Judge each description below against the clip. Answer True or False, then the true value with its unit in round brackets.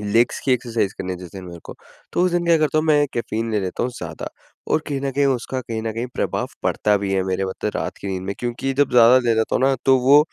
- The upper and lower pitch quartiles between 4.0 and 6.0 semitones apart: True (4.9 semitones)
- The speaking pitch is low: True (120 Hz)